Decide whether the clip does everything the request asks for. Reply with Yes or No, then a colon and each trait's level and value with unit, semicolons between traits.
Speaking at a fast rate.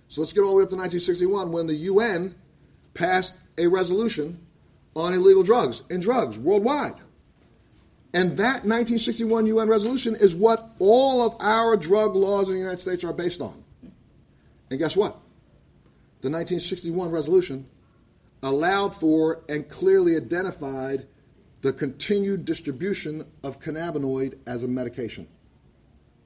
No: slow, 135 wpm